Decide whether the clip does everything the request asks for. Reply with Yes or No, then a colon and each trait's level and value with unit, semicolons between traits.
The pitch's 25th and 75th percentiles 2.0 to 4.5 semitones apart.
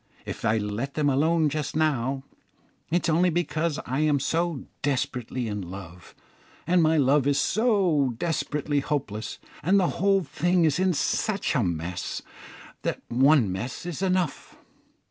No: average, 5.2 semitones